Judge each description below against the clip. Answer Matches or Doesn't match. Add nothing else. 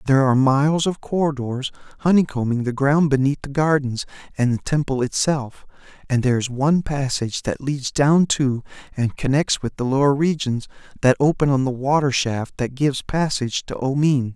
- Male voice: Matches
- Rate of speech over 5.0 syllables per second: Matches